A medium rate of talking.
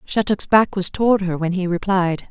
No: fast, 210 wpm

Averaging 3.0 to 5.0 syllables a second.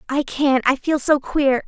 Yes: 4.1 syllables/s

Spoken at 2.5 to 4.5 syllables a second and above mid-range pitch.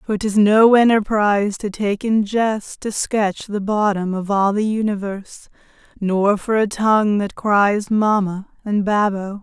Yes: 4.0 syllables/s; high, 205 Hz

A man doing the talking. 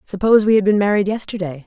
No: female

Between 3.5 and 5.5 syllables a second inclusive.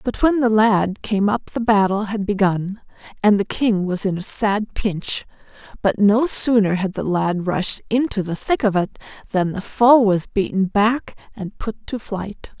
Yes: 4.2 syllables/s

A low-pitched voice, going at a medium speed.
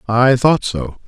Yes: low, 120 Hz; average, 165 wpm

